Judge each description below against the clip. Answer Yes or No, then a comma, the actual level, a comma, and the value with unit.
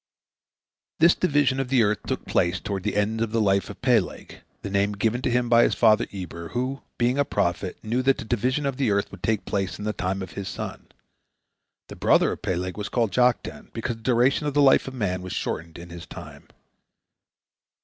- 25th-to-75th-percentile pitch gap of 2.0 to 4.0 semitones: No, average, 4.7 semitones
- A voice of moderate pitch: No, low, 110 Hz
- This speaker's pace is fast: Yes, fast, 215 wpm